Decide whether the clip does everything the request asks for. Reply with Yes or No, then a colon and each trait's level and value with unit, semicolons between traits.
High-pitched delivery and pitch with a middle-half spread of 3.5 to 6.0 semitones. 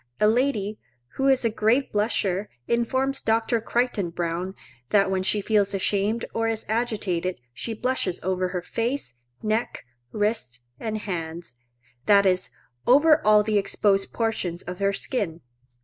Yes: high, 210 Hz; average, 3.8 semitones